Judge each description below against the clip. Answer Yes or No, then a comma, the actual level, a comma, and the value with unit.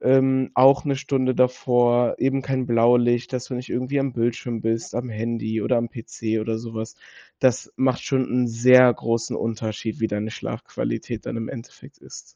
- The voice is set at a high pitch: No, low, 120 Hz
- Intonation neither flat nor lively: No, narrow, 2.1 semitones